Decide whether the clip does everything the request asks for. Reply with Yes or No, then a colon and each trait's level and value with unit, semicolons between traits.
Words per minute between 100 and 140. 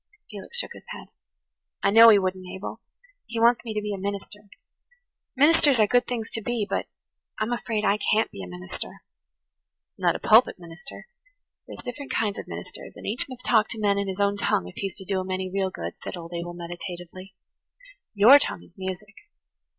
No: average, 200 wpm